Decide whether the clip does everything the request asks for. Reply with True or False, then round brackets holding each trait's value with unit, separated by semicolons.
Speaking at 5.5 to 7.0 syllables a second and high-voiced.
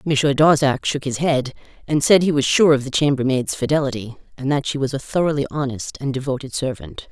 False (5.8 syllables/s; 140 Hz)